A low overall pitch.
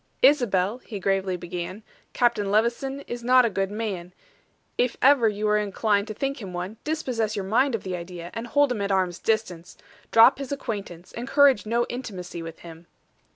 No: high, 215 Hz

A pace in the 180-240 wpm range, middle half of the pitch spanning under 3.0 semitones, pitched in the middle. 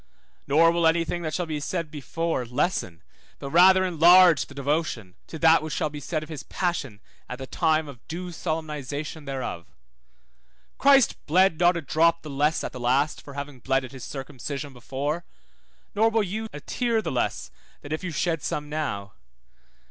No: average, 185 wpm; average, 3.7 semitones; medium, 155 Hz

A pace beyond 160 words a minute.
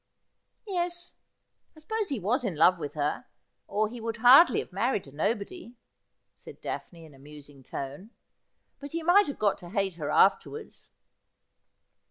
Yes: average, 170 wpm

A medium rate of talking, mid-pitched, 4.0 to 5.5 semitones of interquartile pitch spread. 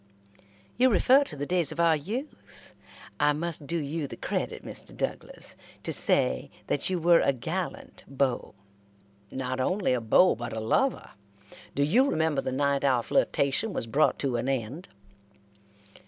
Yes: average, 160 wpm; medium, 145 Hz; average, 4.9 semitones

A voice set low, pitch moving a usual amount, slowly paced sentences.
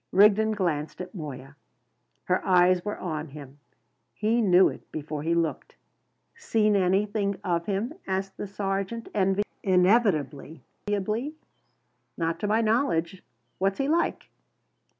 No: high, 190 Hz; average, 4.2 semitones; slow, 120 wpm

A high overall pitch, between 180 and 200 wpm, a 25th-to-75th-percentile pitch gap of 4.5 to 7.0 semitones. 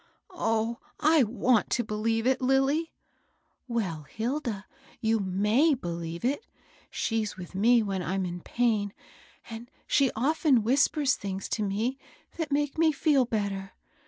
No: high, 230 Hz; average, 155 wpm; average, 5.0 semitones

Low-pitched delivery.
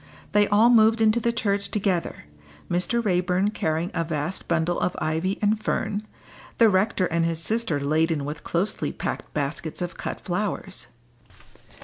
No: medium, 185 Hz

